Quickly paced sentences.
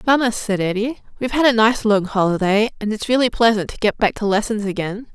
Yes: fast, 220 wpm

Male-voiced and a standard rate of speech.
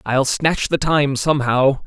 Yes: male; average, 160 wpm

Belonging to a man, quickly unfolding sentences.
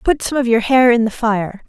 No: female; fast, 285 wpm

